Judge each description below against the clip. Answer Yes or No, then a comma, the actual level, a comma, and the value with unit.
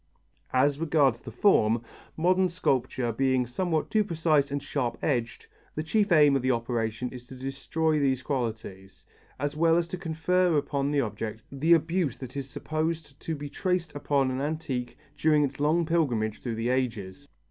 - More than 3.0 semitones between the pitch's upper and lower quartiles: Yes, average, 4.3 semitones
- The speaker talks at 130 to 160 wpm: No, average, 170 wpm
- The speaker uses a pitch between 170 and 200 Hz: No, medium, 140 Hz